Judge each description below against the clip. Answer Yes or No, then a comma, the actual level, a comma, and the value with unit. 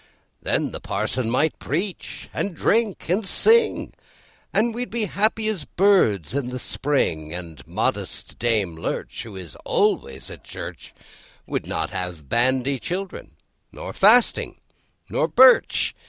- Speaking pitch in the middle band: Yes, medium, 145 Hz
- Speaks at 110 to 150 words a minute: Yes, average, 140 wpm